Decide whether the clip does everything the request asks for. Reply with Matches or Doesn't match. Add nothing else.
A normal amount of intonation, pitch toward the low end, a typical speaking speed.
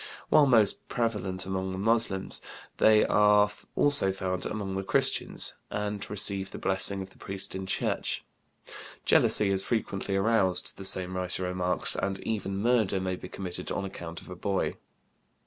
Doesn't match